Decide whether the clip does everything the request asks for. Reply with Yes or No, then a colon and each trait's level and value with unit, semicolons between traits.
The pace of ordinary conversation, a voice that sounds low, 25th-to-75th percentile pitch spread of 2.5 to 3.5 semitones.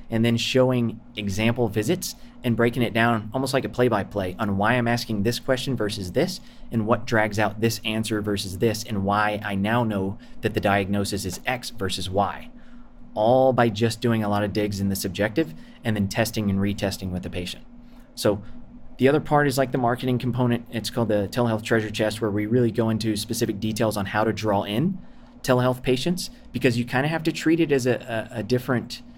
No: fast, 215 wpm; low, 115 Hz; average, 3.0 semitones